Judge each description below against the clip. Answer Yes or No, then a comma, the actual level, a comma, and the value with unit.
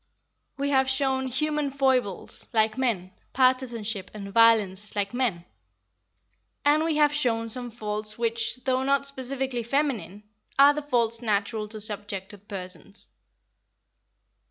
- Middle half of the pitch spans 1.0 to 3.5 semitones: No, average, 4.2 semitones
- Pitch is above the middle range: Yes, high, 235 Hz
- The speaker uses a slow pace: Yes, slow, 125 wpm